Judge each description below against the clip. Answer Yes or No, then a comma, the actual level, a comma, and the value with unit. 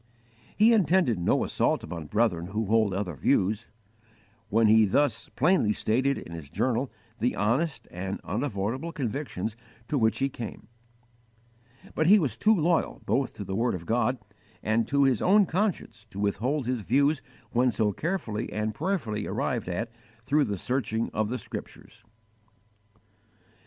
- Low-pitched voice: Yes, low, 115 Hz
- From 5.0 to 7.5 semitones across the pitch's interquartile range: Yes, average, 5.3 semitones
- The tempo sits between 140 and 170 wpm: Yes, average, 150 wpm